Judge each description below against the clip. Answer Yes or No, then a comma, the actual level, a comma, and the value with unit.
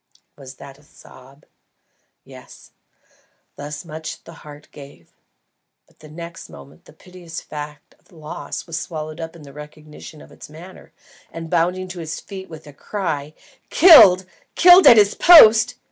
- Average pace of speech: Yes, average, 150 wpm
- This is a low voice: No, medium, 160 Hz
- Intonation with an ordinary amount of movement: Yes, average, 3.5 semitones